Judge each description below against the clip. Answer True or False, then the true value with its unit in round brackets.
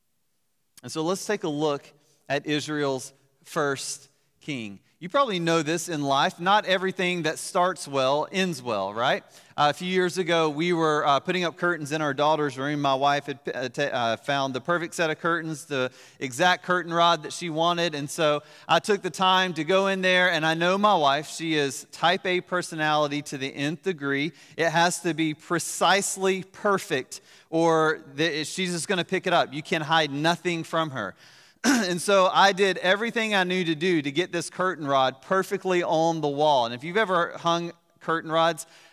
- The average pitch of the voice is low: False (165 Hz)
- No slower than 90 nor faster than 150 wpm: False (195 wpm)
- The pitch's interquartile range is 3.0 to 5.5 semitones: True (3.5 semitones)